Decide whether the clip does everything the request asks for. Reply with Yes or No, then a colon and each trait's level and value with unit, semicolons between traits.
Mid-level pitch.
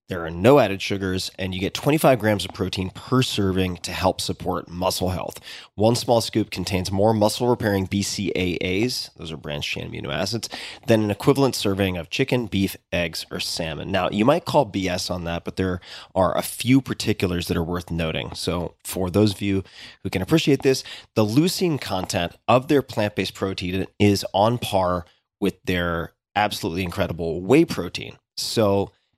No: low, 100 Hz